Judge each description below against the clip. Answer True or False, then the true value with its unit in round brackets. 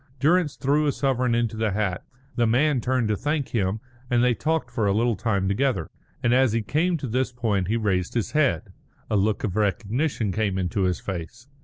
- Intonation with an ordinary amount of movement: True (4.7 semitones)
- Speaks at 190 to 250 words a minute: True (205 wpm)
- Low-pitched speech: True (115 Hz)